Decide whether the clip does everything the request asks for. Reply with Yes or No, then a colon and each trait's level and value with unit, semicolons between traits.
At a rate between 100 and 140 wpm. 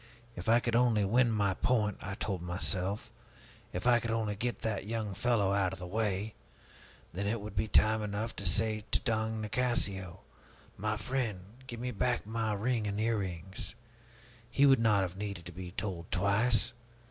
No: average, 180 wpm